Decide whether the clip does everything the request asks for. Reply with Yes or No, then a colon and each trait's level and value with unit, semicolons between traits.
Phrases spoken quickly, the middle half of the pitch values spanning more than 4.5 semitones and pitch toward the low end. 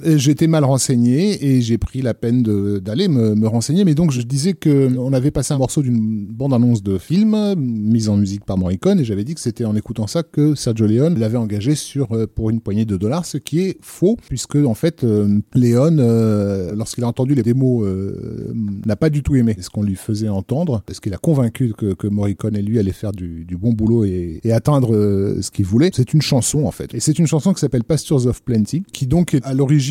Yes: fast, 235 wpm; wide, 5.6 semitones; low, 120 Hz